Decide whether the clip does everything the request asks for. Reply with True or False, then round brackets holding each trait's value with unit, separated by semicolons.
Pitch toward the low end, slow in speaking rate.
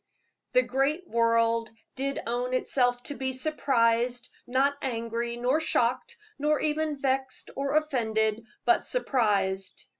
False (255 Hz; 120 wpm)